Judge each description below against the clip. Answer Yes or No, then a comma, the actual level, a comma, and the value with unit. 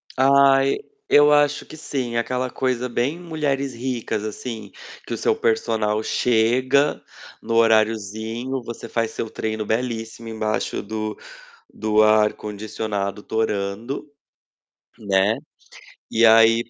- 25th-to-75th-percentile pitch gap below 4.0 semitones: Yes, average, 3.1 semitones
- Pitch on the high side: No, low, 115 Hz